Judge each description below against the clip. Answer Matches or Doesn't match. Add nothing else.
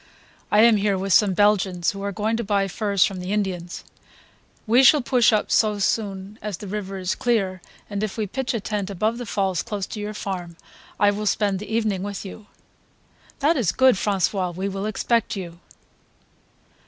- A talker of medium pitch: Doesn't match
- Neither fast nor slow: Matches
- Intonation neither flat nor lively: Doesn't match